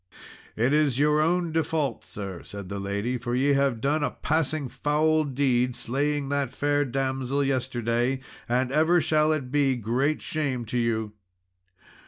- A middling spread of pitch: Yes, average, 3.5 semitones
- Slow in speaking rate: No, average, 160 wpm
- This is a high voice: No, low, 135 Hz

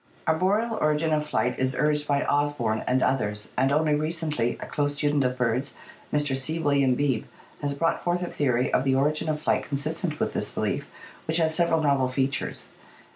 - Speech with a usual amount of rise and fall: Yes, average, 3.0 semitones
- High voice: No, medium, 145 Hz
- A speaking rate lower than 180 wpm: No, average, 185 wpm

